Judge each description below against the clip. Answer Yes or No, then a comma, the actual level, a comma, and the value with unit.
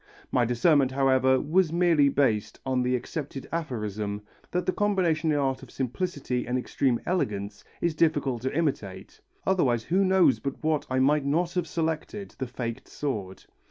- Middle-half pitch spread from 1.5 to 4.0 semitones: No, average, 4.9 semitones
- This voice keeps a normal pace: Yes, average, 160 wpm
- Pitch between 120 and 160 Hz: Yes, medium, 140 Hz